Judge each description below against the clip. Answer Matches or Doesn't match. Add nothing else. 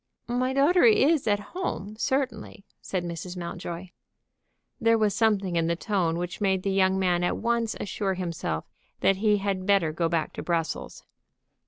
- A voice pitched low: Doesn't match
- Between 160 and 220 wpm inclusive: Matches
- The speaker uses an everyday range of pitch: Matches